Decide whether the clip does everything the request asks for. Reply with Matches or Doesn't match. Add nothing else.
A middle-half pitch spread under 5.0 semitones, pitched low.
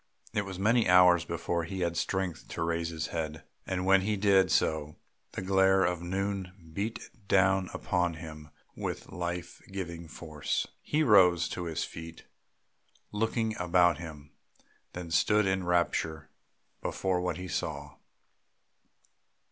Matches